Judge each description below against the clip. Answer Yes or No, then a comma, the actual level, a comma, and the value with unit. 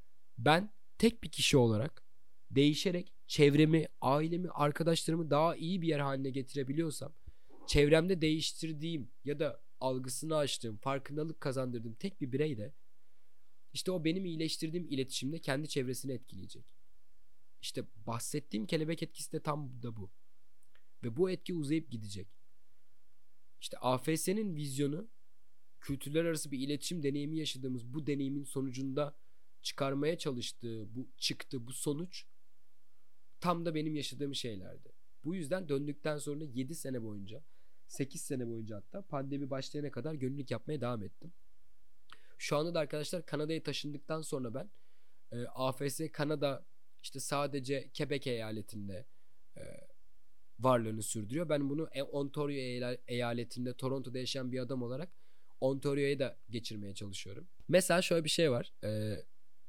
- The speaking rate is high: No, average, 125 wpm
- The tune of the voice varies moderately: Yes, average, 3.9 semitones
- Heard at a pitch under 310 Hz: Yes, medium, 140 Hz